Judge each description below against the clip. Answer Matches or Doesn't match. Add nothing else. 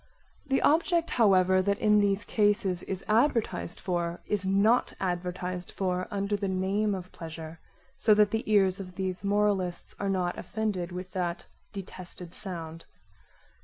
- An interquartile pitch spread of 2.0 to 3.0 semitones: Matches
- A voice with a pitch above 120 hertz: Matches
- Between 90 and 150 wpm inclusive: Matches